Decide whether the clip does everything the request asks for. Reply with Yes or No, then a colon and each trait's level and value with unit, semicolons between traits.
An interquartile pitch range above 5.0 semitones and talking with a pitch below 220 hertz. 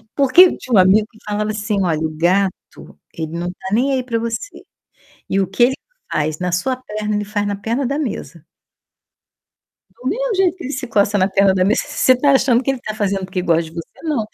Yes: wide, 5.4 semitones; high, 210 Hz